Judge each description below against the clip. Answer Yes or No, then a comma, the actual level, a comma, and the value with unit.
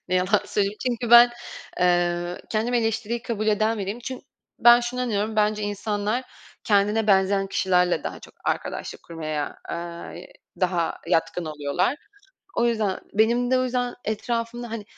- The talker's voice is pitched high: Yes, high, 210 Hz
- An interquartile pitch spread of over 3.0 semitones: Yes, average, 4.4 semitones